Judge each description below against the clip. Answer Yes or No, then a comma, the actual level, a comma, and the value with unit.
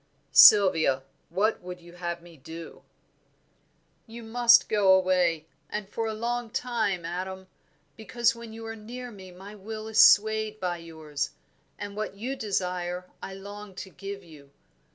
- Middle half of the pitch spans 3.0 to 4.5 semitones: Yes, average, 3.8 semitones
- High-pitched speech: Yes, high, 195 Hz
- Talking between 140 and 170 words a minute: Yes, average, 155 wpm